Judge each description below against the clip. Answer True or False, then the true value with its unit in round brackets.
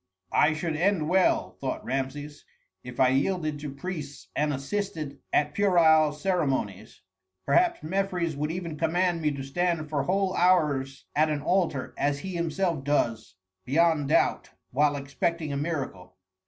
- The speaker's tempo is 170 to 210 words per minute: False (145 wpm)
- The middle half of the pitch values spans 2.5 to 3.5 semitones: False (3.9 semitones)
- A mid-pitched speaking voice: True (155 Hz)